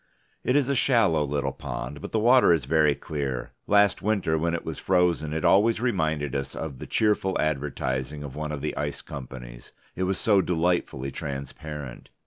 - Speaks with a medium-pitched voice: No, very low, 80 Hz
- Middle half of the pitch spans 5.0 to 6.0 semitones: Yes, average, 5.3 semitones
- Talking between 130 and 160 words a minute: No, average, 180 wpm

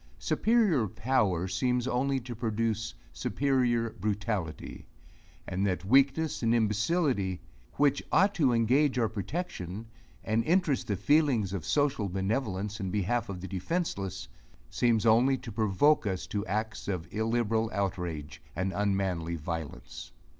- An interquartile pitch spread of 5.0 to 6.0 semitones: Yes, average, 5.3 semitones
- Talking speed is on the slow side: Yes, slow, 130 wpm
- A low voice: Yes, low, 110 Hz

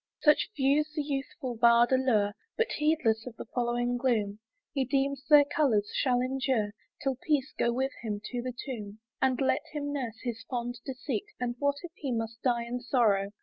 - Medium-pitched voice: No, very high, 255 Hz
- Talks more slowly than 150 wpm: No, average, 185 wpm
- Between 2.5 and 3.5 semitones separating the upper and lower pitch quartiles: Yes, average, 2.9 semitones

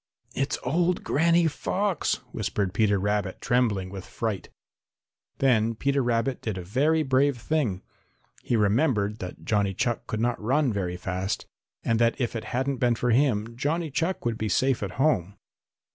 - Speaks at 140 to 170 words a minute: Yes, average, 160 wpm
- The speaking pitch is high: No, low, 120 Hz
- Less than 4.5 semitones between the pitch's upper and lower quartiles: No, average, 5.1 semitones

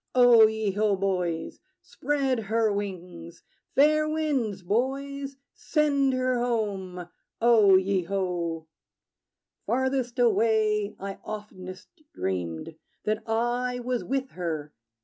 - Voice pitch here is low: No, high, 215 Hz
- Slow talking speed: Yes, slow, 105 wpm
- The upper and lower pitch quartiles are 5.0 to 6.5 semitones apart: Yes, average, 5.3 semitones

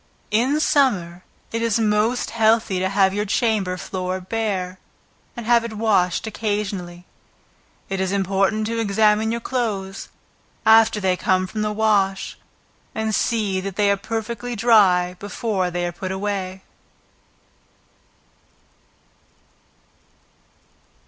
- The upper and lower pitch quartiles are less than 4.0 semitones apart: Yes, average, 2.9 semitones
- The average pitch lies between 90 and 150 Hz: No, high, 205 Hz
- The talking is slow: Yes, slow, 120 wpm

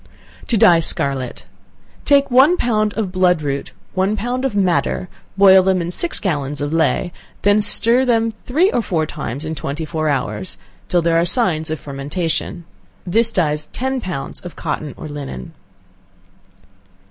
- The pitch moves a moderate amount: No, wide, 6.5 semitones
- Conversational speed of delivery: Yes, average, 160 wpm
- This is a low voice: No, medium, 180 Hz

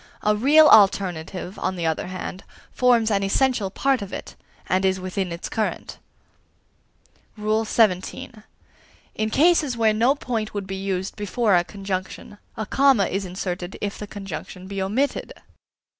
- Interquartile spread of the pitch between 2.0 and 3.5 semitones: Yes, average, 3.1 semitones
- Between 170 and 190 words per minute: No, average, 145 wpm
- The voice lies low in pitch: No, high, 200 Hz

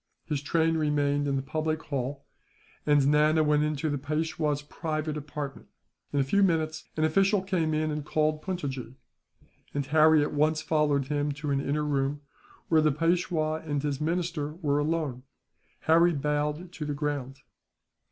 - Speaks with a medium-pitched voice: Yes, medium, 150 Hz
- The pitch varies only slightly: Yes, narrow, 1.6 semitones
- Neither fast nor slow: Yes, average, 160 wpm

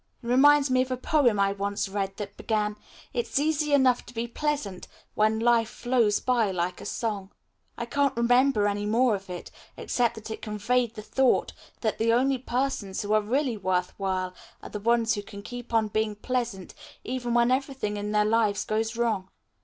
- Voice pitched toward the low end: No, high, 225 Hz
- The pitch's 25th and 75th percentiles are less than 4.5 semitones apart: Yes, average, 3.3 semitones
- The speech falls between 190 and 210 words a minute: Yes, average, 195 wpm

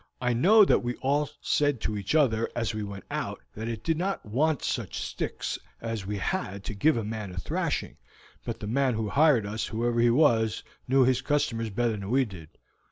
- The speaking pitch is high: No, low, 115 Hz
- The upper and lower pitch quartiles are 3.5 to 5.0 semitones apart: Yes, average, 4.3 semitones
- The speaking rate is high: Yes, fast, 210 wpm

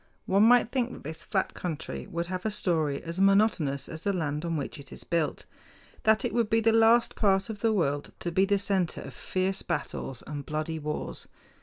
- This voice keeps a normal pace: No, fast, 210 wpm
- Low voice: No, medium, 185 Hz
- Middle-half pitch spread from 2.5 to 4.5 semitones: No, wide, 5.4 semitones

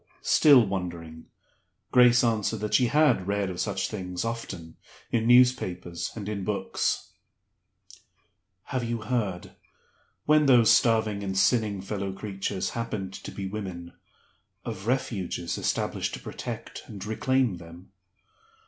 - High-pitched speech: No, low, 105 Hz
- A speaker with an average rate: No, slow, 125 wpm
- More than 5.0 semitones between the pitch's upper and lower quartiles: No, average, 3.9 semitones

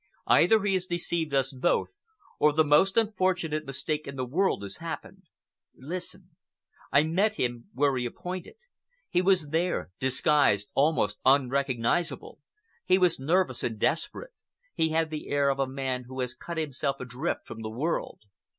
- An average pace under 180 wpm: Yes, average, 160 wpm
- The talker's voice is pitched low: No, medium, 150 Hz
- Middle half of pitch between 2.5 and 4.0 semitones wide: No, average, 5.0 semitones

